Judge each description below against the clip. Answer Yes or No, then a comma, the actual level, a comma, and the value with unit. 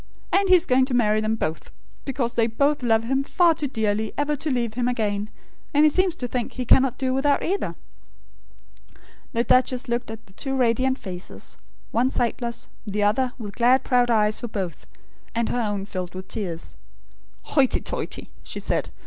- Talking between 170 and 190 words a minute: Yes, average, 185 wpm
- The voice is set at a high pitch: Yes, high, 240 Hz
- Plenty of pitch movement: No, average, 3.6 semitones